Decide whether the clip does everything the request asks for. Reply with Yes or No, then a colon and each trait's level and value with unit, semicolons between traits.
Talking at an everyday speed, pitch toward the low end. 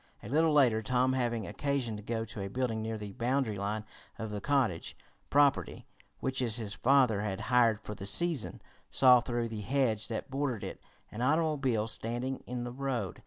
Yes: average, 180 wpm; low, 120 Hz